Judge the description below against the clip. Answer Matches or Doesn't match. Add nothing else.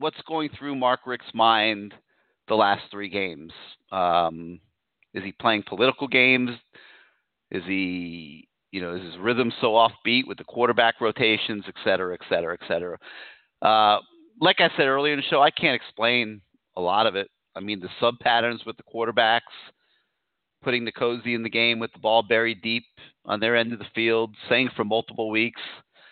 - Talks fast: Doesn't match